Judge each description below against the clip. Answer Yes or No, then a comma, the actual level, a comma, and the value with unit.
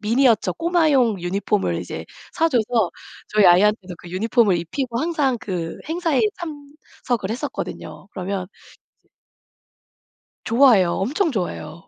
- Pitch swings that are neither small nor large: No, wide, 6.8 semitones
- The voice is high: Yes, high, 225 Hz